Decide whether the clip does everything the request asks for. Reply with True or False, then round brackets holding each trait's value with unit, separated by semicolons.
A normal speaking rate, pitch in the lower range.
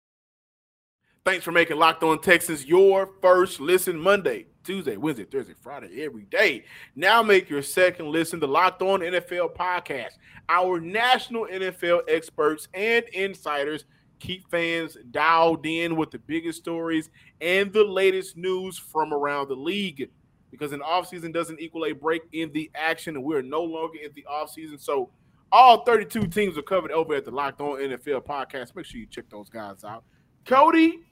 False (170 wpm; 170 Hz)